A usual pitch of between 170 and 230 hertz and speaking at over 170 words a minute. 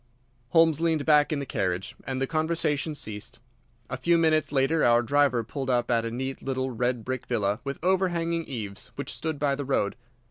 No: low, 135 Hz; average, 190 wpm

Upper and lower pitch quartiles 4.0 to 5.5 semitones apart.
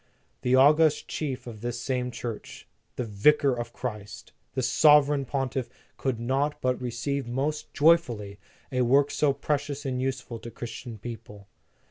No: average, 3.2 semitones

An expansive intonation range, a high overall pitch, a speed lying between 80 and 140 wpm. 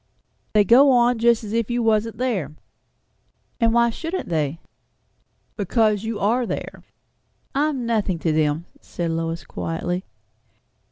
Yes: wide, 5.7 semitones; high, 220 Hz; slow, 135 wpm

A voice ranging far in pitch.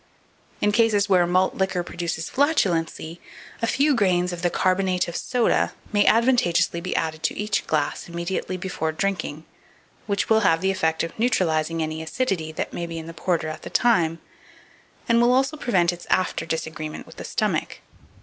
No: average, 4.1 semitones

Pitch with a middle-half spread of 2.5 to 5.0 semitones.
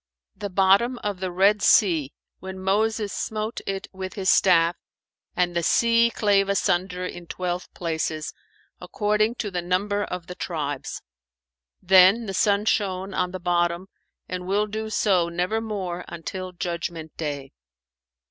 Yes: average, 2.9 semitones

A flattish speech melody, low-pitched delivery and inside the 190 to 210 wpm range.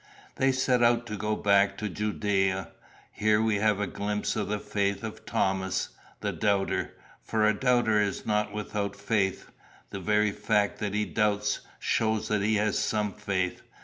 No: narrow, 1.1 semitones; low, 105 Hz; average, 170 wpm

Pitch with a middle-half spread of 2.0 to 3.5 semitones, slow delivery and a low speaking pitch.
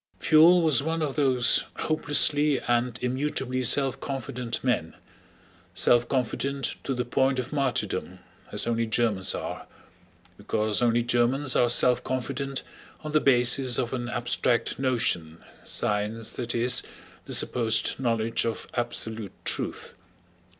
Yes: average, 2.7 semitones; slow, 125 wpm; low, 125 Hz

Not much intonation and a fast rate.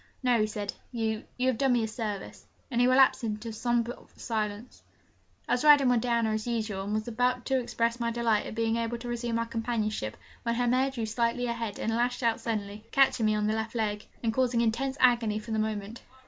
Yes: narrow, 2.1 semitones; fast, 225 wpm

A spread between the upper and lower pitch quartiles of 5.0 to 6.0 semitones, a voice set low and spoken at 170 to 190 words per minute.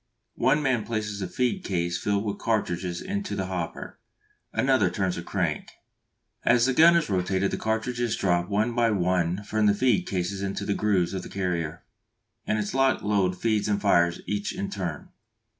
No: average, 3.7 semitones; low, 100 Hz; average, 175 wpm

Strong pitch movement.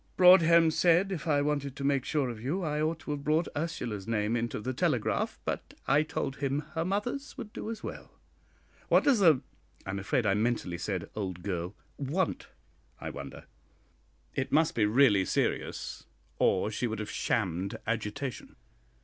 Yes: wide, 7.2 semitones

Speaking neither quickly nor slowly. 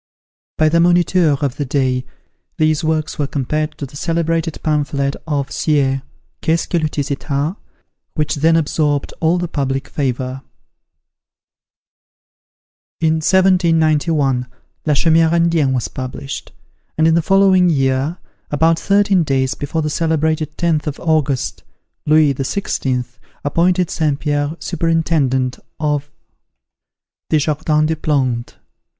No: slow, 125 wpm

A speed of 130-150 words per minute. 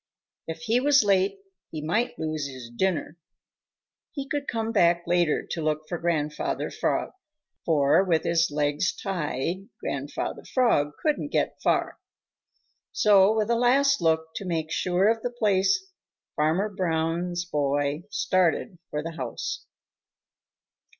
Yes: slow, 135 wpm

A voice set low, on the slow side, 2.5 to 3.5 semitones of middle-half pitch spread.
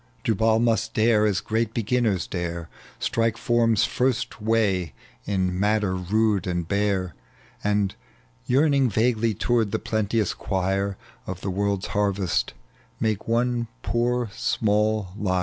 Yes: low, 105 Hz; slow, 125 wpm; average, 2.9 semitones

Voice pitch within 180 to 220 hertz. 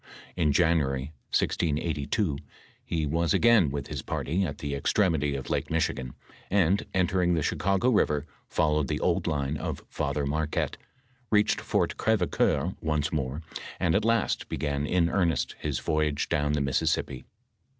No: very low, 80 Hz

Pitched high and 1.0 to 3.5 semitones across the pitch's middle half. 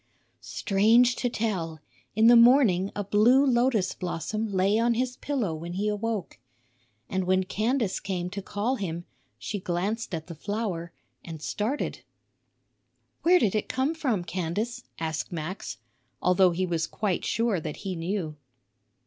No: high, 200 Hz; average, 4.7 semitones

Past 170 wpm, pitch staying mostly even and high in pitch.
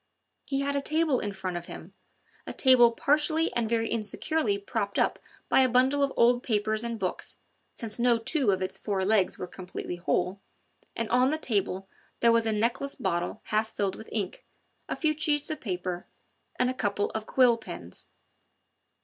No: average, 185 wpm; average, 4.6 semitones; high, 230 Hz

